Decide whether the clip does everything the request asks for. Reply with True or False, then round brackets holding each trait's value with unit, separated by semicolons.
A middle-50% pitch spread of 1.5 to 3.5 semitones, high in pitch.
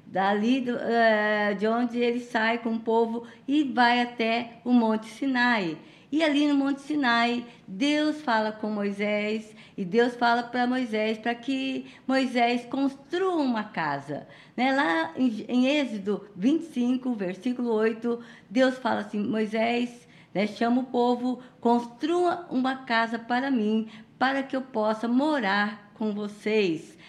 True (3.0 semitones; 235 Hz)